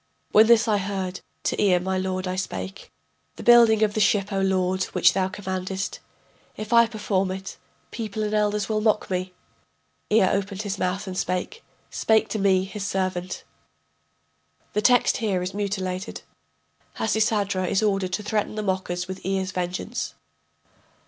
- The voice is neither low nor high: No, high, 195 Hz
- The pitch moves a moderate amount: No, narrow, 2.2 semitones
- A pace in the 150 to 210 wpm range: Yes, average, 160 wpm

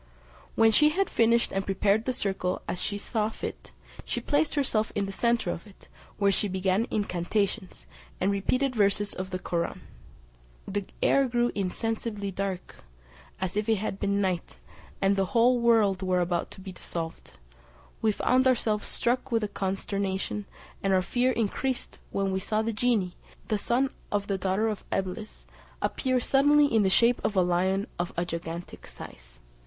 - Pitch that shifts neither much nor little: Yes, average, 3.5 semitones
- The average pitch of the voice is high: Yes, high, 205 Hz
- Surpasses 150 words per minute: Yes, average, 170 wpm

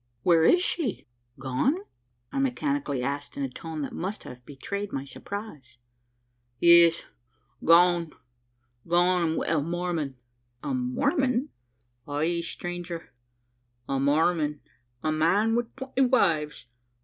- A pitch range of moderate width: No, wide, 6.4 semitones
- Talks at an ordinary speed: No, slow, 120 wpm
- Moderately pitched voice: Yes, medium, 170 Hz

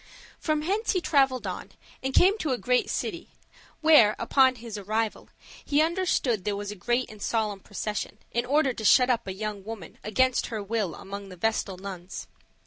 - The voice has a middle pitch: No, high, 225 Hz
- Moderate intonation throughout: Yes, average, 4.5 semitones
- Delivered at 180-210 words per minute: Yes, average, 185 wpm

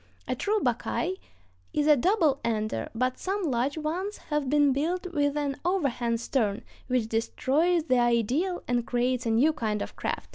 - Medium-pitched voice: No, very high, 275 Hz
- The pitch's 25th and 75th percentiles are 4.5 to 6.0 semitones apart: Yes, average, 5.1 semitones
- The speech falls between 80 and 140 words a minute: No, average, 170 wpm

